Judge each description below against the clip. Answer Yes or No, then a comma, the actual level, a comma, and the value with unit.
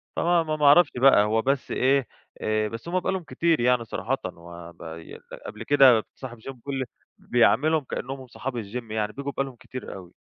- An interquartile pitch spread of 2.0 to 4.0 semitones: No, average, 4.4 semitones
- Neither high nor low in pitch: No, low, 125 Hz